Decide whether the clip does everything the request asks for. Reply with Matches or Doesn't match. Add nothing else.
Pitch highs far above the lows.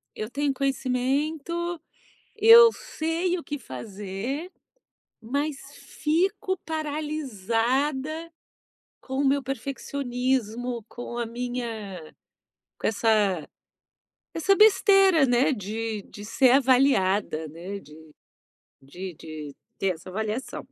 Matches